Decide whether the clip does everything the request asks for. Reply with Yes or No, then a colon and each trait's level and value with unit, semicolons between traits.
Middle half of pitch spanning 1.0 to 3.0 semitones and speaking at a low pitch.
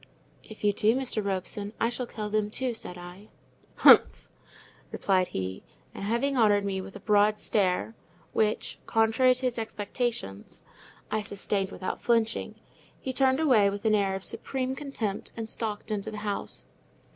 No: average, 2.7 semitones; high, 215 Hz